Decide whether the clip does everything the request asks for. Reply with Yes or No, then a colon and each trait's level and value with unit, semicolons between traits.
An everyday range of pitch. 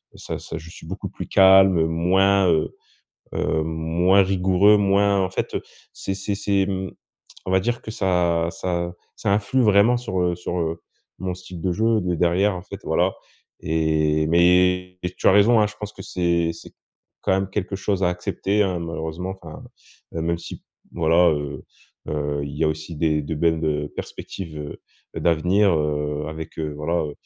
Yes: average, 3.1 semitones